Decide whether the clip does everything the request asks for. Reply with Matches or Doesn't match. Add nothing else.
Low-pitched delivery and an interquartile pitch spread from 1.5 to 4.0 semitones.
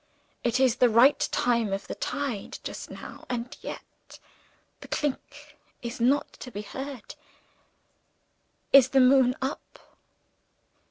Doesn't match